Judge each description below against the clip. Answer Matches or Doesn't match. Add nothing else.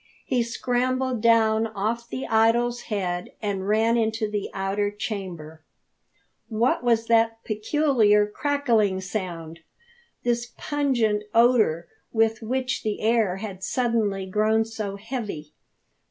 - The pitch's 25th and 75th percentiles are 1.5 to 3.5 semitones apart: Matches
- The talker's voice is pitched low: Doesn't match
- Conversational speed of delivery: Doesn't match